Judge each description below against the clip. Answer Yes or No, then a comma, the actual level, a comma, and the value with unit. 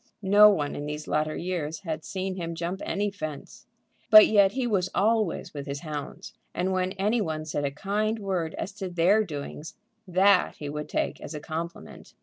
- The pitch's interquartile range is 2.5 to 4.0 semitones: No, average, 4.5 semitones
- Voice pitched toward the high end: No, medium, 180 Hz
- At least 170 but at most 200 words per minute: Yes, average, 190 wpm